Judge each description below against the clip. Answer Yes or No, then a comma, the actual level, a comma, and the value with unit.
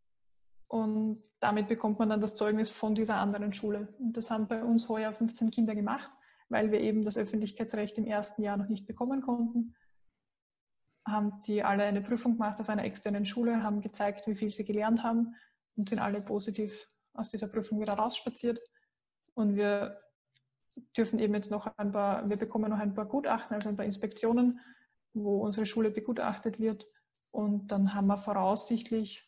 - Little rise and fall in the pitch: Yes, narrow, 1.6 semitones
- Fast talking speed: No, average, 175 wpm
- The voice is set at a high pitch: Yes, high, 215 Hz